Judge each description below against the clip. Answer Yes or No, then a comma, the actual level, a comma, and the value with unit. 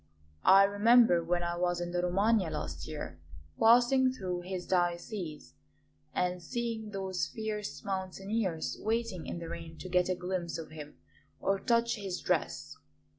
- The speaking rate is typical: Yes, average, 150 wpm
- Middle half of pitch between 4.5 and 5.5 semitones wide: No, average, 3.9 semitones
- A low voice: No, medium, 185 Hz